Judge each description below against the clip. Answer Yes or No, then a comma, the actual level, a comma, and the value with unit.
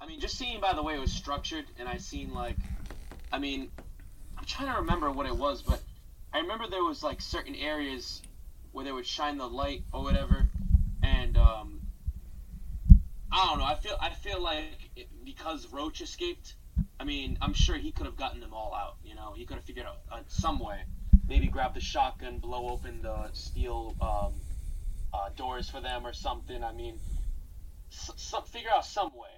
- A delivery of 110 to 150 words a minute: No, average, 200 wpm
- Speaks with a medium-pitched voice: No, very low, 95 Hz